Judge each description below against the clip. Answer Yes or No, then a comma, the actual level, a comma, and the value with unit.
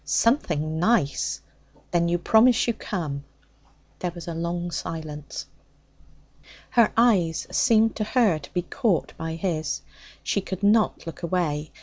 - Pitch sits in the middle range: Yes, medium, 175 Hz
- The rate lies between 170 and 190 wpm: No, slow, 135 wpm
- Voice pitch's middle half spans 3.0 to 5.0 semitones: No, wide, 5.4 semitones